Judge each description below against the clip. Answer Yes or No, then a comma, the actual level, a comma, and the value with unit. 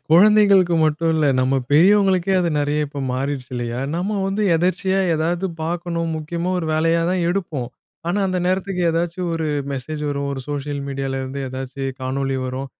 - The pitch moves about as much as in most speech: Yes, average, 4.6 semitones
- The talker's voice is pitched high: No, medium, 160 Hz